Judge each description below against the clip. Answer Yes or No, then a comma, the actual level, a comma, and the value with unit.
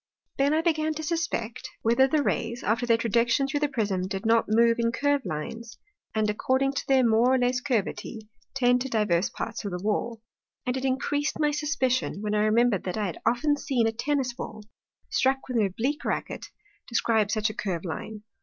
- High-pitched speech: Yes, high, 235 Hz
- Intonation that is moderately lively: Yes, average, 3.9 semitones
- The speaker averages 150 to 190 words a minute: No, average, 200 wpm